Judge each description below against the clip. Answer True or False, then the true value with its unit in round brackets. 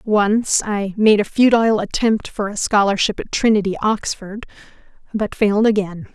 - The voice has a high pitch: True (210 Hz)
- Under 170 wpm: True (135 wpm)